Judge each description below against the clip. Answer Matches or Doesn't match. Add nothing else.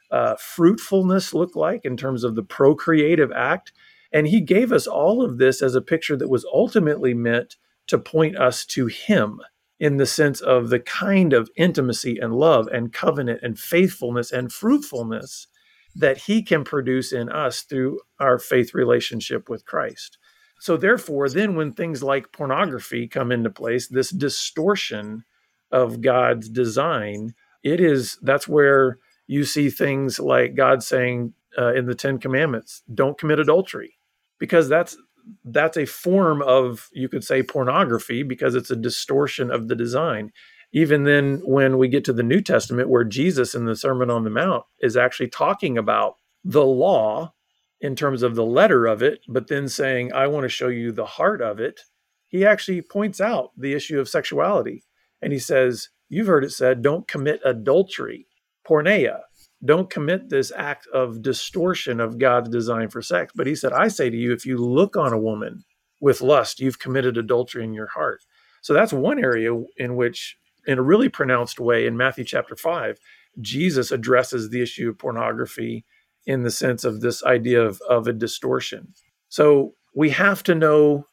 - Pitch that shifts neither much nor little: Matches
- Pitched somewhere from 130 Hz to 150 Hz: Matches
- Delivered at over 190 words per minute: Doesn't match